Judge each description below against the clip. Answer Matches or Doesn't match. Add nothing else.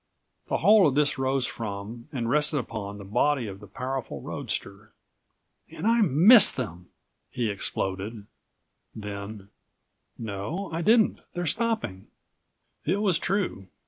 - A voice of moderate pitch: Doesn't match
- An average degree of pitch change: Doesn't match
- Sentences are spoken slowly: Matches